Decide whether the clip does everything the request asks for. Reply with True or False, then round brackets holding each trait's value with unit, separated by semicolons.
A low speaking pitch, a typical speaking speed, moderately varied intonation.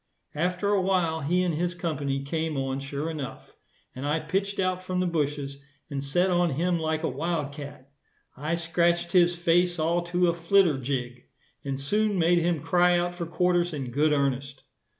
False (165 Hz; 185 wpm; 3.8 semitones)